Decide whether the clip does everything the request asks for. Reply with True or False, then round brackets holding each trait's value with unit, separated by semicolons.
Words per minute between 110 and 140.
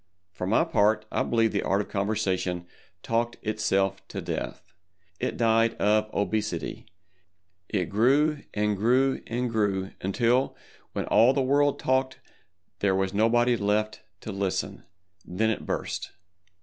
True (135 wpm)